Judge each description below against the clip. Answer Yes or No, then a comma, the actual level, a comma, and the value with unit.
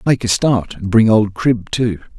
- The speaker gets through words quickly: Yes, fast, 220 wpm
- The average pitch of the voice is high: No, low, 110 Hz